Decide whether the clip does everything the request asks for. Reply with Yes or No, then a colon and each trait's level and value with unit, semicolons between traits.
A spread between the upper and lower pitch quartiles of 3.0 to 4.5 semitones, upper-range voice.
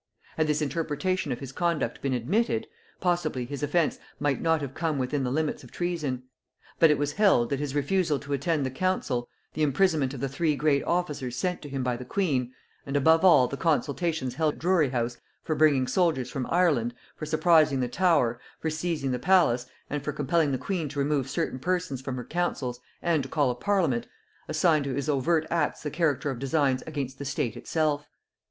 No: average, 3.9 semitones; medium, 145 Hz